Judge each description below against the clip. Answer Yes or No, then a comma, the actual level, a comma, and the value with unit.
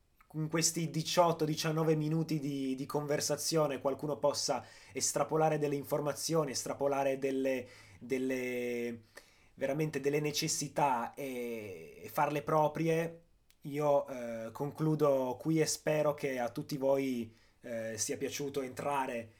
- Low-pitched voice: No, medium, 145 Hz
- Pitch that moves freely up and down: No, average, 2.7 semitones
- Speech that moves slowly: Yes, slow, 110 wpm